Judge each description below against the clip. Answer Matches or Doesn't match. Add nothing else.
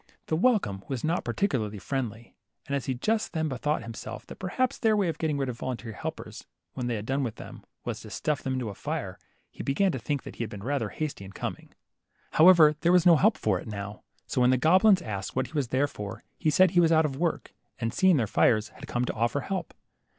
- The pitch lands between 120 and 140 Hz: Matches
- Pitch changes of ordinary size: Doesn't match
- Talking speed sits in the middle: Doesn't match